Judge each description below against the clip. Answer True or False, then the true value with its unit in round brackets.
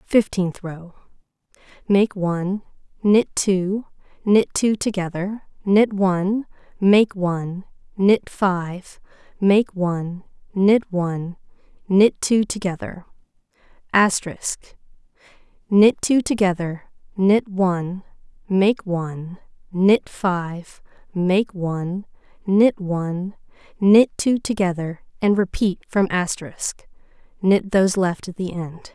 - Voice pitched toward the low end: False (190 Hz)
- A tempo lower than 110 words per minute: True (100 wpm)